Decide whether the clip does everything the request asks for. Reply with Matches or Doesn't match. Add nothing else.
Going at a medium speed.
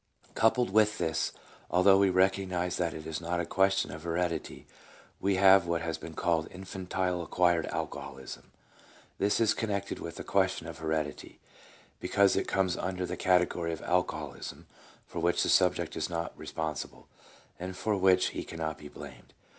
Matches